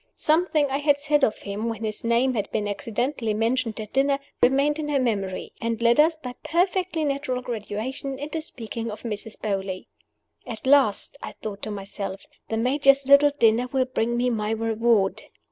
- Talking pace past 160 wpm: Yes, average, 180 wpm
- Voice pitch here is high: Yes, high, 240 Hz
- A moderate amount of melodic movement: Yes, average, 4.5 semitones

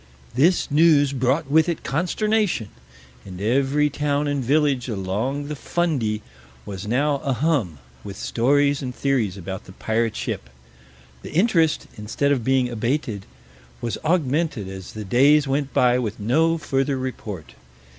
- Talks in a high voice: No, low, 135 Hz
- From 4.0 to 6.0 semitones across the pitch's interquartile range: Yes, average, 5.1 semitones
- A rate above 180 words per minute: No, average, 140 wpm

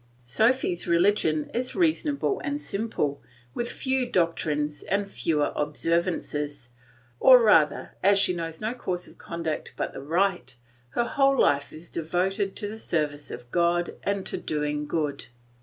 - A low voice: No, medium, 170 Hz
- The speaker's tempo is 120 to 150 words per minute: Yes, average, 145 wpm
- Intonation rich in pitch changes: Yes, wide, 6.2 semitones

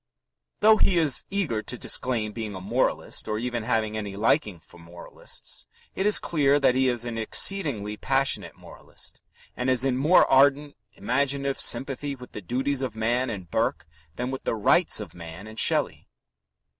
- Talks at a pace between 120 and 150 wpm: No, average, 170 wpm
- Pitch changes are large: No, average, 4.3 semitones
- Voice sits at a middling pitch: No, low, 125 Hz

